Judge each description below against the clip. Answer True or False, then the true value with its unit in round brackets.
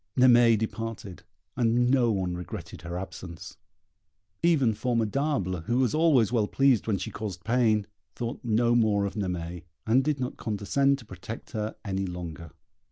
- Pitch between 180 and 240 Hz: False (110 Hz)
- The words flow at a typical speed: True (155 wpm)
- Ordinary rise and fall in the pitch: True (4.4 semitones)